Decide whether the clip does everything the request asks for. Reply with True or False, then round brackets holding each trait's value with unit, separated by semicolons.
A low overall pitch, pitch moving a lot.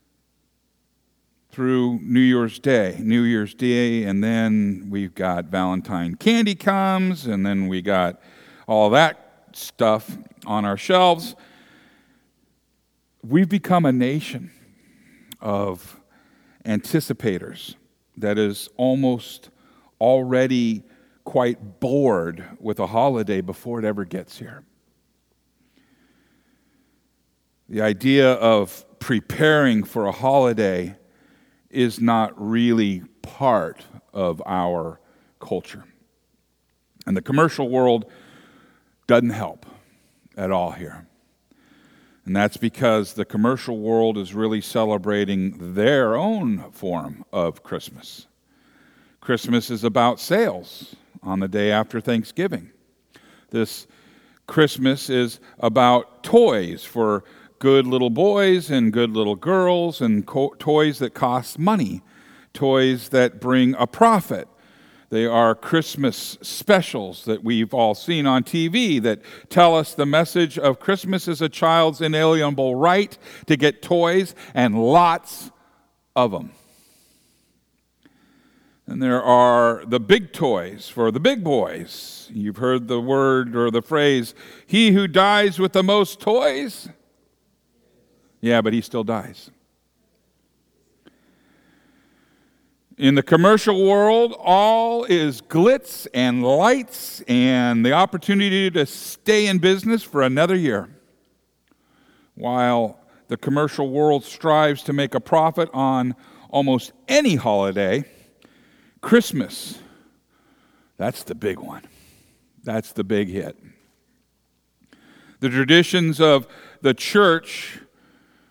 True (130 Hz; 8.0 semitones)